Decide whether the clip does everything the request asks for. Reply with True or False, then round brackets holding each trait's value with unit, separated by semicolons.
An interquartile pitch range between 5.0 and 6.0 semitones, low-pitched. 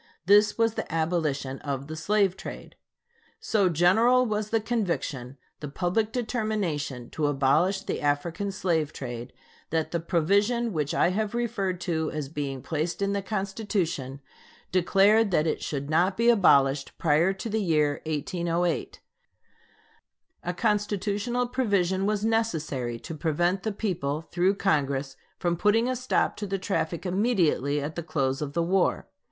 False (5.5 semitones; 175 Hz)